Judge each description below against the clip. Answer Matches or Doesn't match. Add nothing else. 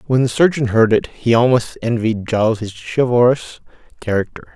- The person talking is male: Matches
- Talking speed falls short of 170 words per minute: Matches